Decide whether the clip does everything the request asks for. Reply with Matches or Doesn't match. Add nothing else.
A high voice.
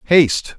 Doesn't match